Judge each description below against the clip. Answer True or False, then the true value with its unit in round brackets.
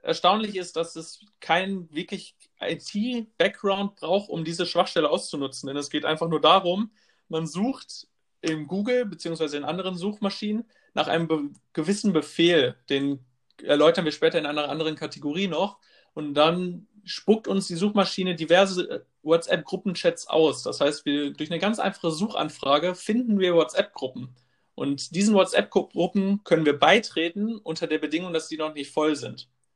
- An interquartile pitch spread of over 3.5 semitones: True (4.3 semitones)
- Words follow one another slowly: False (155 wpm)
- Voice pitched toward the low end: False (170 Hz)